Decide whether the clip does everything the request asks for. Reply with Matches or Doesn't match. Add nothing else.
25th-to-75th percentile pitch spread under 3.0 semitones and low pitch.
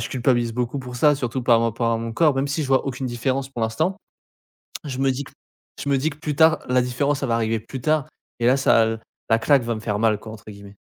Doesn't match